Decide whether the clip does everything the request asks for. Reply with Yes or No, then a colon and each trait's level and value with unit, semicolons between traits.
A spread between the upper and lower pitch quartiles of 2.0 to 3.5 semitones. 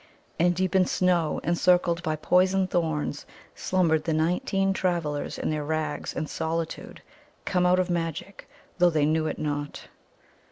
Yes: narrow, 2.6 semitones